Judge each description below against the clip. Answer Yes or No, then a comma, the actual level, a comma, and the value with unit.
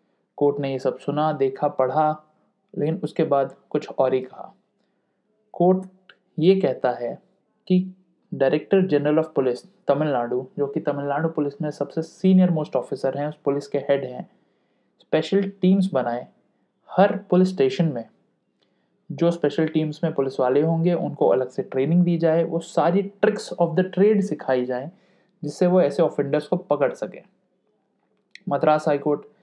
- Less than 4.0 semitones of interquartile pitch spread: No, average, 4.6 semitones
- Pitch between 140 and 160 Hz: Yes, medium, 155 Hz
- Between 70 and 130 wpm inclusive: No, average, 155 wpm